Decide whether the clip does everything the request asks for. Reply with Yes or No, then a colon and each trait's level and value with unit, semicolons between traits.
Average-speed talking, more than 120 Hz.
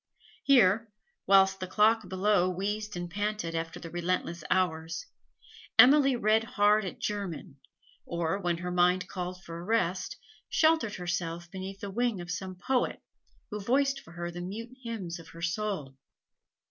Yes: average, 150 wpm; high, 190 Hz